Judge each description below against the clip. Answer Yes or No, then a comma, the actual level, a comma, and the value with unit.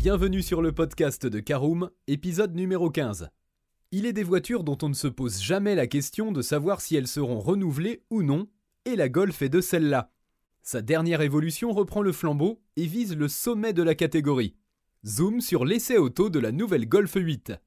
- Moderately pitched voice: Yes, medium, 165 Hz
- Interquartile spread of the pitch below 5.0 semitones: No, average, 5.3 semitones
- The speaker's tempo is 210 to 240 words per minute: No, average, 195 wpm